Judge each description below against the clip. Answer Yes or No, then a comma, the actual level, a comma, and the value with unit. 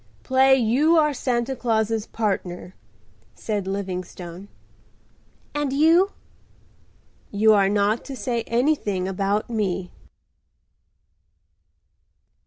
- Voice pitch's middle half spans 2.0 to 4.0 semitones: No, average, 5.1 semitones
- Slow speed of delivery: Yes, slow, 85 wpm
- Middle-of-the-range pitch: No, high, 220 Hz